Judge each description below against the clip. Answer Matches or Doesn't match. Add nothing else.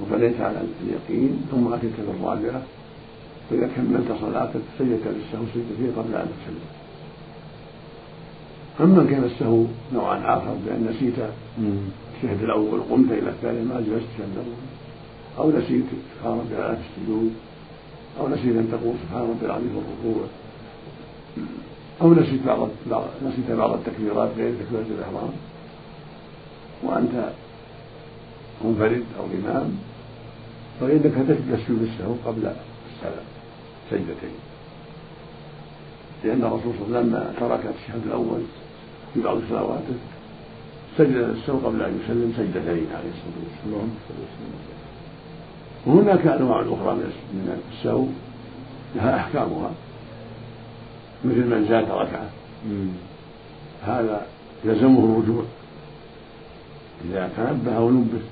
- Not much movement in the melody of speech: Matches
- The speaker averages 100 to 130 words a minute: Matches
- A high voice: Doesn't match